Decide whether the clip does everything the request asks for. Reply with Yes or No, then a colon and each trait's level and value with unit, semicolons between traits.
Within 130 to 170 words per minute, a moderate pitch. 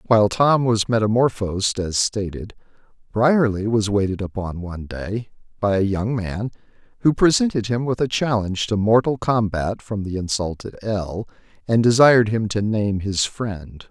No: average, 155 wpm; low, 105 Hz